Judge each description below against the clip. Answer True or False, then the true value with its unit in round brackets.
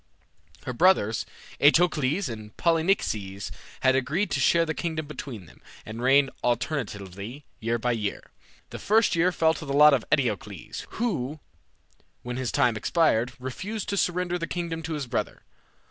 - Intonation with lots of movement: True (6.0 semitones)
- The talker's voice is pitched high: False (140 Hz)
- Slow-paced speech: False (155 wpm)